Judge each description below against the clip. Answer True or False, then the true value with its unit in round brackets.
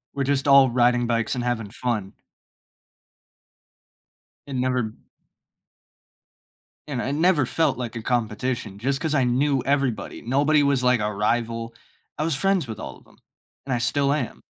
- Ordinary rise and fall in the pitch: True (3.2 semitones)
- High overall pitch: False (125 Hz)